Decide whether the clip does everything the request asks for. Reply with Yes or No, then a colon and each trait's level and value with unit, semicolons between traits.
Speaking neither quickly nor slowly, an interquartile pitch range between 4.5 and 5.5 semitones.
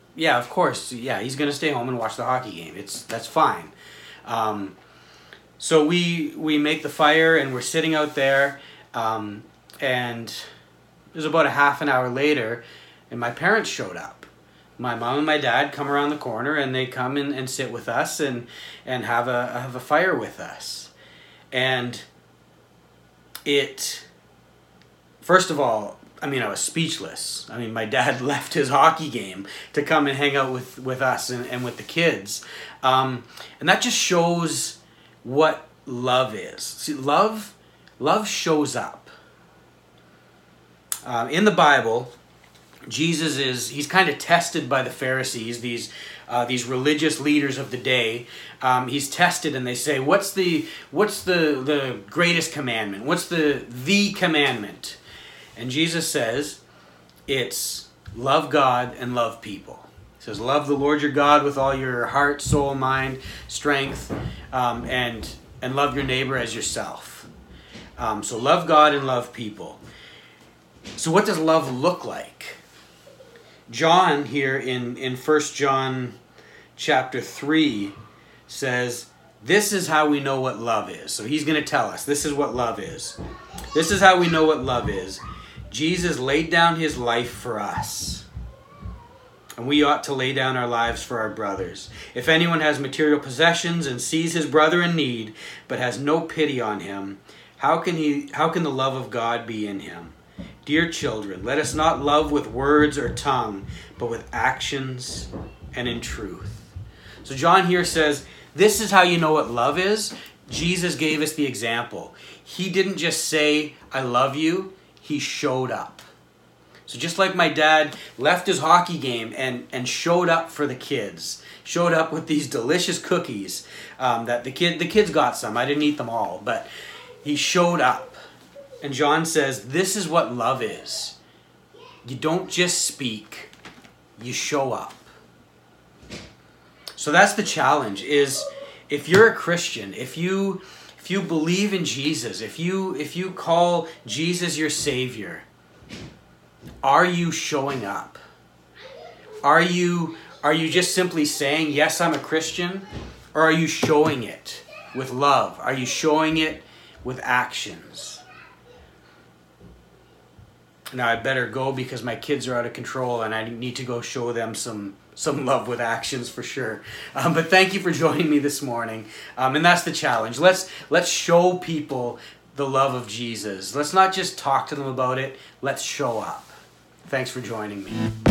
Yes: average, 165 wpm; average, 4.8 semitones